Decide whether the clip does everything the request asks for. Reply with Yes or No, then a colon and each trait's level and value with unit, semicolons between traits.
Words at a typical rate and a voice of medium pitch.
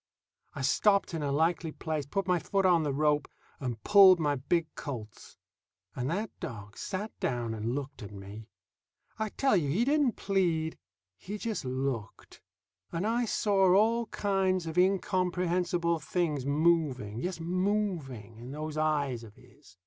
Yes: average, 155 wpm; medium, 165 Hz